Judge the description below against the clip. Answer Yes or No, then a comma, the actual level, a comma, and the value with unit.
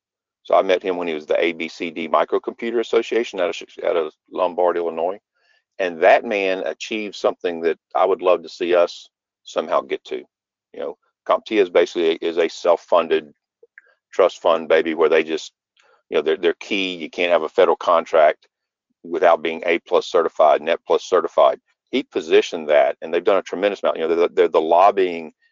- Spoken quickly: No, average, 185 wpm